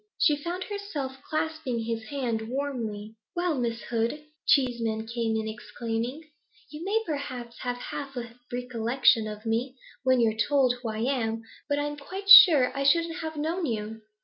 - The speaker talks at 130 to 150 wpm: No, average, 160 wpm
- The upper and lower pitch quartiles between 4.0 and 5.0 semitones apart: Yes, average, 4.4 semitones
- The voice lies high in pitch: Yes, very high, 250 Hz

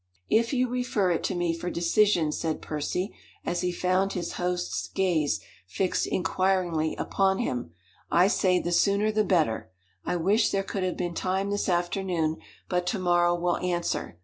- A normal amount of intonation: No, narrow, 2.0 semitones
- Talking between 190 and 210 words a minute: No, average, 170 wpm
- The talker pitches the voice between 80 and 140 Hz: No, medium, 180 Hz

